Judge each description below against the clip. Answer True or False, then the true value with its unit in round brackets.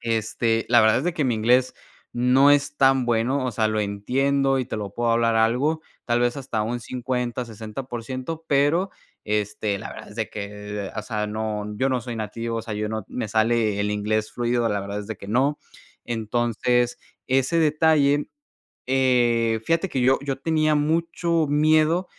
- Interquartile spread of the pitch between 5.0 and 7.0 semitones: False (3.9 semitones)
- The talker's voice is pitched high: False (120 Hz)